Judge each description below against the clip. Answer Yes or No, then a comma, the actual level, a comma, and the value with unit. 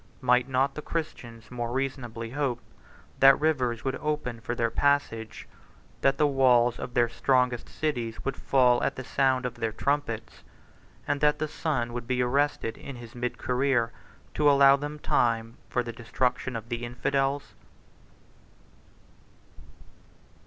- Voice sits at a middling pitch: No, low, 125 Hz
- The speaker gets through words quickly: No, average, 150 wpm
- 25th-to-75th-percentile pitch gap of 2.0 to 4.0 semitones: Yes, average, 2.7 semitones